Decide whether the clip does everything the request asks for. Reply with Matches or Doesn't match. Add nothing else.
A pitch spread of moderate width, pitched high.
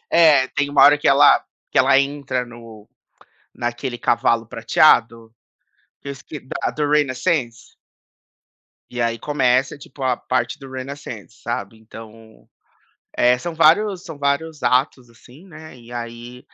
Doesn't match